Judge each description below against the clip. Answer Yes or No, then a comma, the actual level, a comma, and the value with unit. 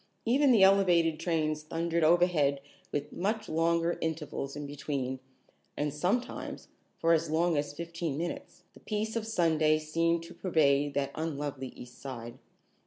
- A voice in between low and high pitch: Yes, medium, 160 Hz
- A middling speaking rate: Yes, average, 145 wpm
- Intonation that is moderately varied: Yes, average, 3.0 semitones